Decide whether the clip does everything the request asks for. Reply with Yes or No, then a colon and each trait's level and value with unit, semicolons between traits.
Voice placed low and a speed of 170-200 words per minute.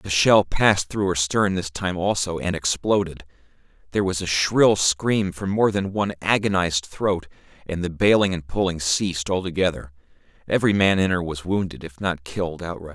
Yes: very low, 90 Hz; average, 180 wpm